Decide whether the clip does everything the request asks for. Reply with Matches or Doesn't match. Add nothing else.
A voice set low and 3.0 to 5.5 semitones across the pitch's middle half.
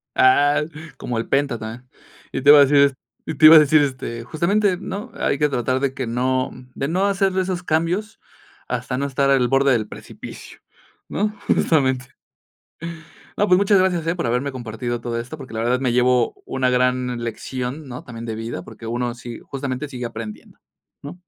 Matches